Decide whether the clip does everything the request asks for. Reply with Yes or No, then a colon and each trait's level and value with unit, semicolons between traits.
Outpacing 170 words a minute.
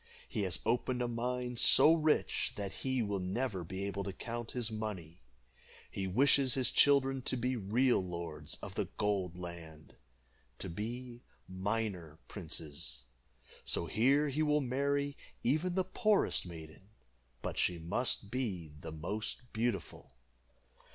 No: average, 140 wpm